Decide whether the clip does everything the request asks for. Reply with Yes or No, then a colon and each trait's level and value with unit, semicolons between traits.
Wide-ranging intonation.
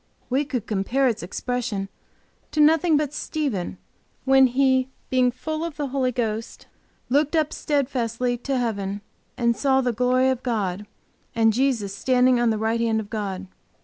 No: average, 3.4 semitones